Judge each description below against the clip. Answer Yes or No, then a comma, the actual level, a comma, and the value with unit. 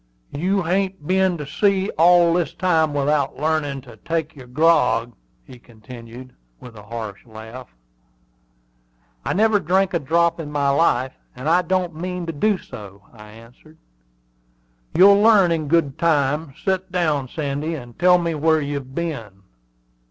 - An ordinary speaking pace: Yes, average, 150 wpm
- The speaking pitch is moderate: Yes, medium, 155 Hz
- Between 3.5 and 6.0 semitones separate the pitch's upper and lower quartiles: Yes, wide, 5.5 semitones